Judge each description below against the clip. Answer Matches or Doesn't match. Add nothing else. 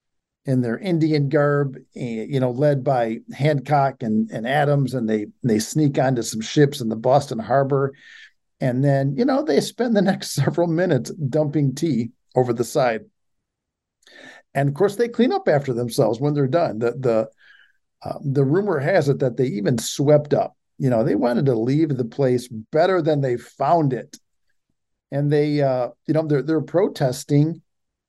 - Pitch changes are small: Doesn't match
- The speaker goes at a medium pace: Matches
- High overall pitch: Doesn't match